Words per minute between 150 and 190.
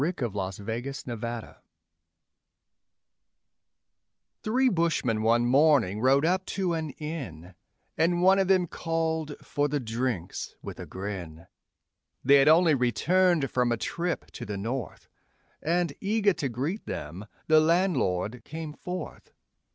No: slow, 135 wpm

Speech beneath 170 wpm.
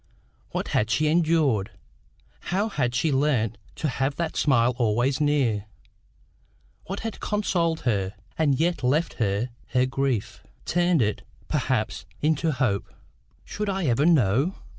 Yes: slow, 135 wpm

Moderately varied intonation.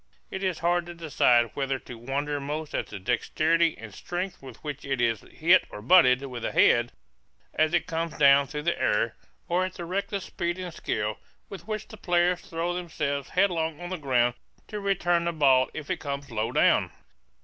Yes: average, 4.8 semitones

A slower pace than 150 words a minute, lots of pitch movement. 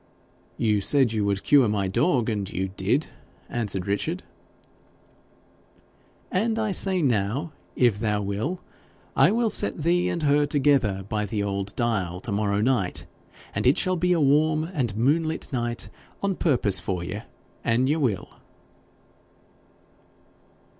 Yes: average, 140 wpm; wide, 7.2 semitones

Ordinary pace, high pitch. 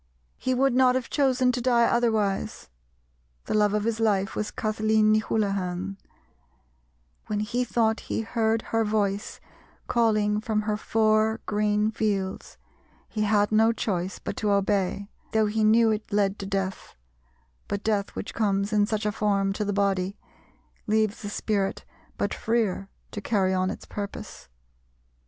Yes: average, 155 wpm; high, 210 Hz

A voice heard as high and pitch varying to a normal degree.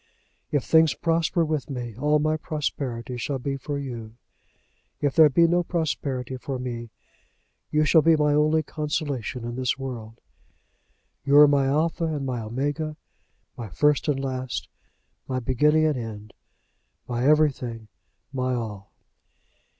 No: medium, 140 Hz; average, 3.8 semitones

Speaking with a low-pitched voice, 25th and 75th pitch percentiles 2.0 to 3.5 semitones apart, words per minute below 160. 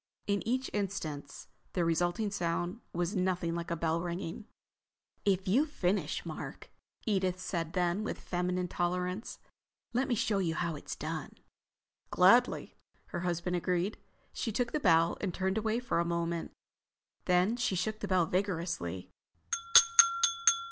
No: medium, 180 Hz; average, 2.9 semitones; average, 140 wpm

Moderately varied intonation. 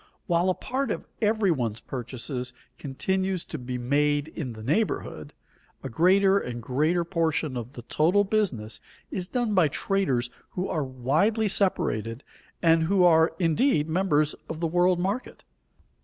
No: wide, 6.7 semitones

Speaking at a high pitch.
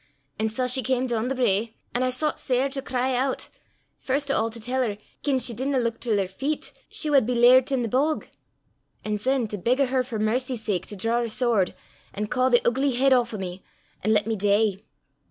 Yes: high, 245 Hz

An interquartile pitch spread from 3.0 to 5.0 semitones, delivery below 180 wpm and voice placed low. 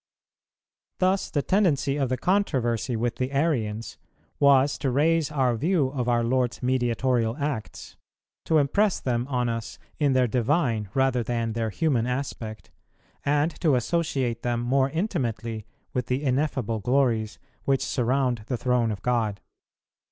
Yes: average, 3.3 semitones; average, 145 wpm; low, 125 Hz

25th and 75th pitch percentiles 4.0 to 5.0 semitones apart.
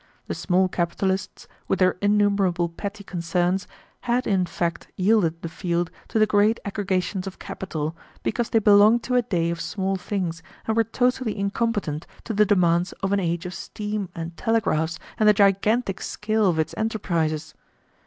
No: average, 3.5 semitones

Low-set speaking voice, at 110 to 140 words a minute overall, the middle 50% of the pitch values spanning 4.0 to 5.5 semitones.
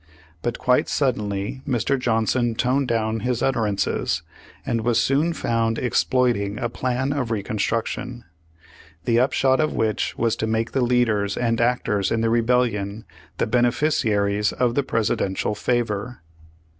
No: low, 115 Hz; slow, 135 wpm; narrow, 2.5 semitones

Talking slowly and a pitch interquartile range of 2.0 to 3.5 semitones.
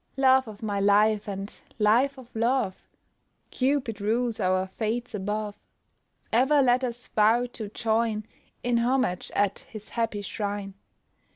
Yes: slow, 130 wpm; average, 3.1 semitones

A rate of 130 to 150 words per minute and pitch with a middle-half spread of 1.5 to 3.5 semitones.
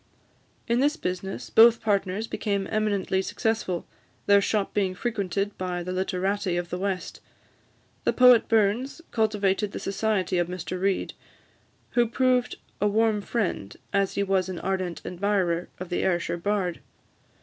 Yes: average, 145 wpm; average, 2.9 semitones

